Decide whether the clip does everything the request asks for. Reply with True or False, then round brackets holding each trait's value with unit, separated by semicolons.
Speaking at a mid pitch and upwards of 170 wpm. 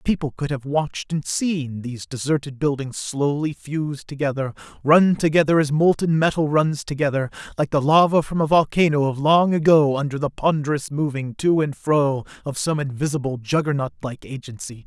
False (145 Hz; 160 wpm)